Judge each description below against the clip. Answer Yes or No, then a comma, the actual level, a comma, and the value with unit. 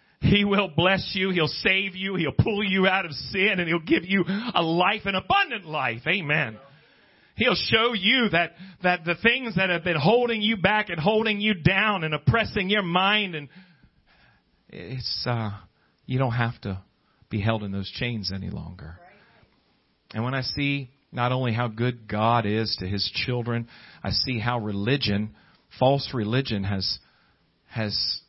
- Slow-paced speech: No, average, 170 wpm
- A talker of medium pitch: Yes, medium, 145 Hz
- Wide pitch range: Yes, wide, 8.6 semitones